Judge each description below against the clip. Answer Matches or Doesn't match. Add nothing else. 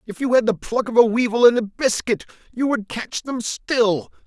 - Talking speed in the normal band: Doesn't match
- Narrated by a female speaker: Doesn't match